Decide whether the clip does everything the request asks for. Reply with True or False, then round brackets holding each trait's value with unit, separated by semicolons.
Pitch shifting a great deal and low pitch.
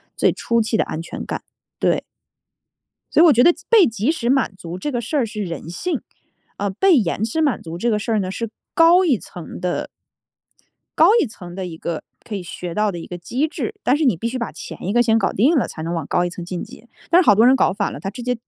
False (6.6 semitones; 220 Hz)